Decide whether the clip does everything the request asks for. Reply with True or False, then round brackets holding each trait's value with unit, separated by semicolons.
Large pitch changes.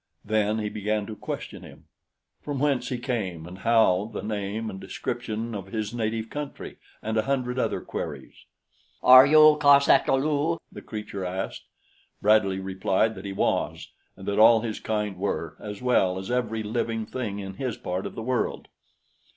False (3.6 semitones)